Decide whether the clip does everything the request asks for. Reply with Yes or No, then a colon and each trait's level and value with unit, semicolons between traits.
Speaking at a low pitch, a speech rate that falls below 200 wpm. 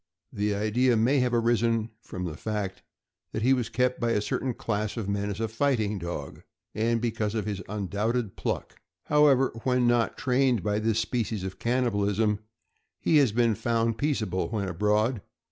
Yes: low, 110 Hz; average, 170 wpm